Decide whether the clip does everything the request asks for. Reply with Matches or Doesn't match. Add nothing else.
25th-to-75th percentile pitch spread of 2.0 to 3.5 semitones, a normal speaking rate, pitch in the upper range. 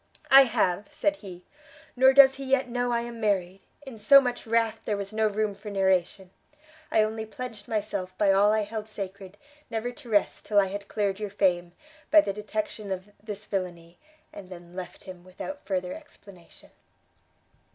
Matches